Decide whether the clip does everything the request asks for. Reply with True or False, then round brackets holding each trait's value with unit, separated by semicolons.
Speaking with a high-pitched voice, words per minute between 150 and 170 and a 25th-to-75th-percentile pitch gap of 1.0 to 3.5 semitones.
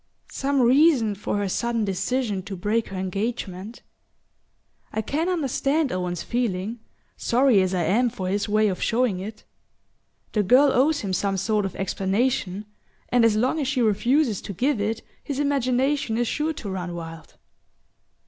False (220 Hz; 160 wpm; 4.9 semitones)